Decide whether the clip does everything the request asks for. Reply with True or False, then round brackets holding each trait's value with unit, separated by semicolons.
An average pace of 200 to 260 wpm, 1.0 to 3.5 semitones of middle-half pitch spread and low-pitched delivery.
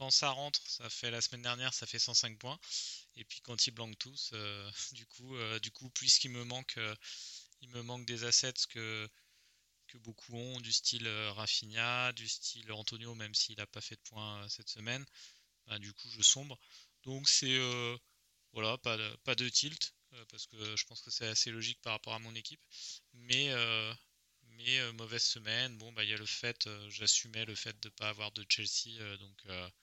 True (215 wpm; 2.4 semitones; 115 Hz)